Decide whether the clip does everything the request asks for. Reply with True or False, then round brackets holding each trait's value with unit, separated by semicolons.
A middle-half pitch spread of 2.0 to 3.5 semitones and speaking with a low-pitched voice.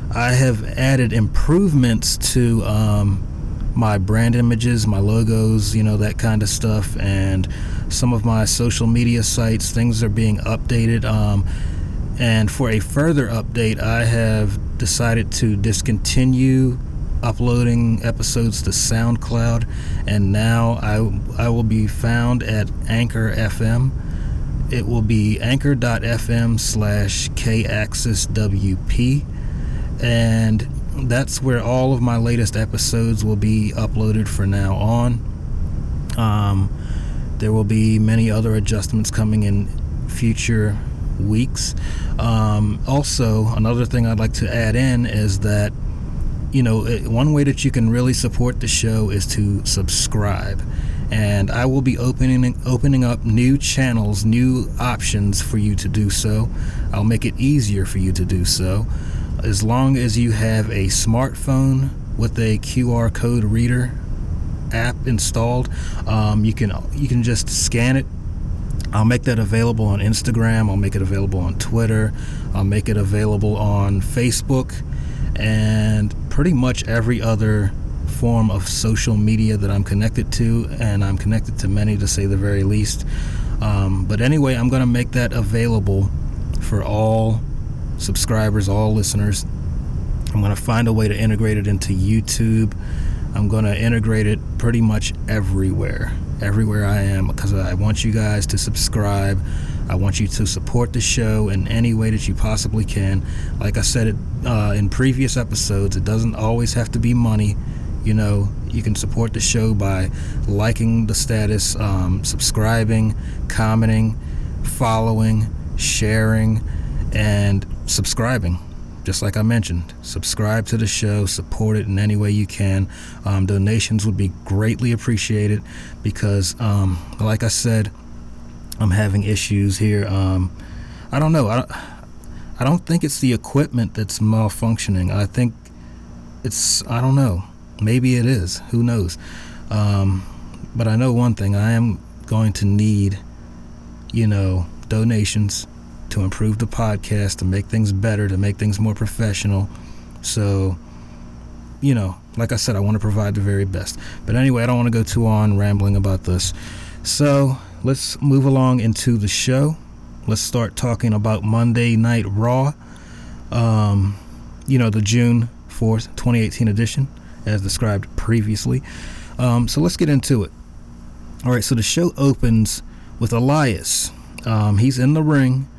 True (3.0 semitones; 110 Hz)